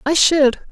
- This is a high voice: Yes, very high, 295 Hz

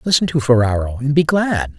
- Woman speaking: No, male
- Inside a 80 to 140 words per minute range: No, average, 200 wpm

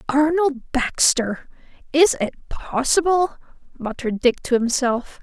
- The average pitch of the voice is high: Yes, very high, 275 Hz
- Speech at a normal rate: No, slow, 105 wpm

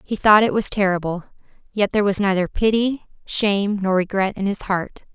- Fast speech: No, average, 185 wpm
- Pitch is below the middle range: No, high, 200 Hz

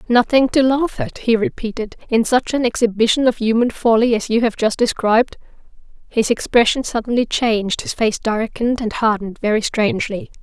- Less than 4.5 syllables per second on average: No, 5.5 syllables/s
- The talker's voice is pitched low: No, high, 225 Hz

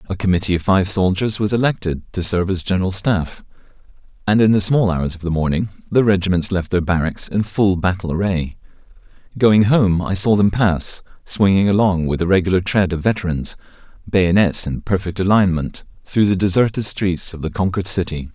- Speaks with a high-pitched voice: No, very low, 95 Hz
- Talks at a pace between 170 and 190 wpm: Yes, average, 180 wpm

